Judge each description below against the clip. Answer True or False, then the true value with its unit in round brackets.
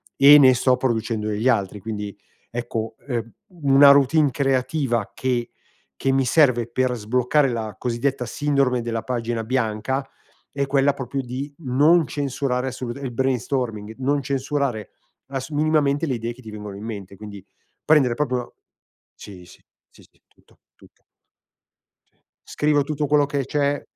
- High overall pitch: False (130 Hz)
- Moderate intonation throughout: True (3.4 semitones)